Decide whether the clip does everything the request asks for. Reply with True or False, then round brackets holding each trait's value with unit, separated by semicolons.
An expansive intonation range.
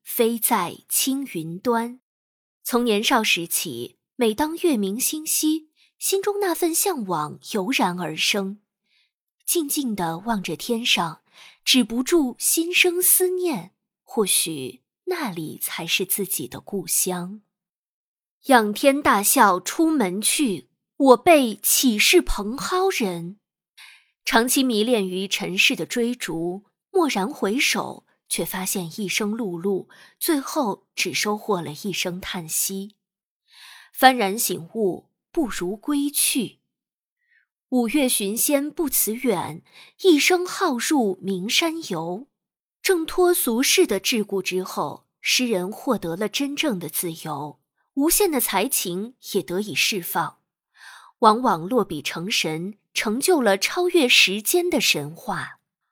True (7.5 semitones)